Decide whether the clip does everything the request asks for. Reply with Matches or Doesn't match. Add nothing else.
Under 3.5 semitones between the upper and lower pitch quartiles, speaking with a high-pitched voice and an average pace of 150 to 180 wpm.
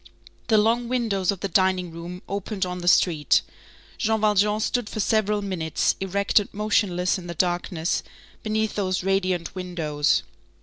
Matches